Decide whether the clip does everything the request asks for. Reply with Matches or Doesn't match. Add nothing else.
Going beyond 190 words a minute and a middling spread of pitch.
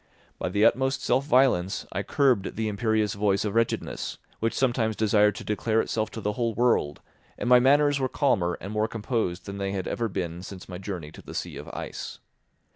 Matches